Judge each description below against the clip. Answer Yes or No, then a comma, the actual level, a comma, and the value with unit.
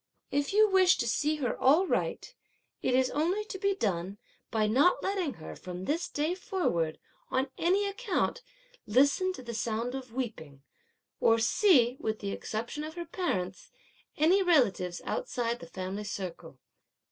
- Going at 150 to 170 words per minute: Yes, average, 160 wpm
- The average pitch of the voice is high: Yes, very high, 260 Hz